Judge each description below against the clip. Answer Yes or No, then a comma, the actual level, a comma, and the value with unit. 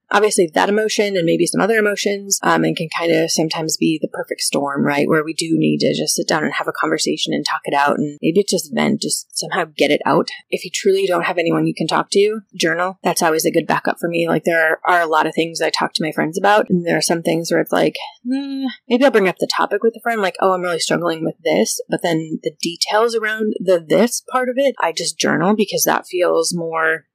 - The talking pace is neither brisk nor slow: No, fast, 260 wpm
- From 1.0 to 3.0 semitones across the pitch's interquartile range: No, average, 4.7 semitones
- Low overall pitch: No, medium, 180 Hz